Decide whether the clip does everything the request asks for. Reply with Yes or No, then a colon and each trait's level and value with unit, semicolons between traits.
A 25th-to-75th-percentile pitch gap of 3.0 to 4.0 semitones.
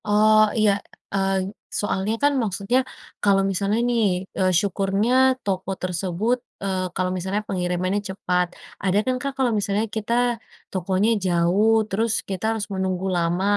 No: narrow, 2.4 semitones